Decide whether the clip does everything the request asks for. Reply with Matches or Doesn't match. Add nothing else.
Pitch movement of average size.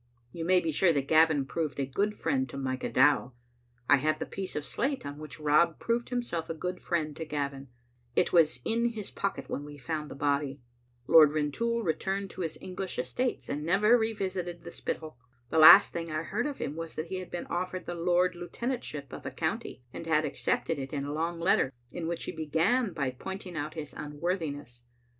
Matches